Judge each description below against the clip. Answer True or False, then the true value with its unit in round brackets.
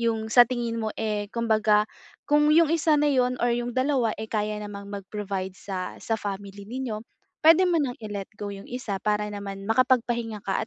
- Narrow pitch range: False (3.6 semitones)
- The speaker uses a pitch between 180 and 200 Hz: False (220 Hz)